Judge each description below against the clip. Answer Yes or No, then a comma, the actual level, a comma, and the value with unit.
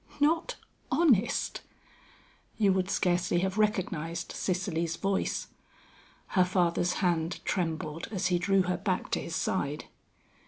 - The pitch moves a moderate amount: No, narrow, 2.3 semitones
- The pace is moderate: No, slow, 120 wpm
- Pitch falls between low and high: Yes, medium, 180 Hz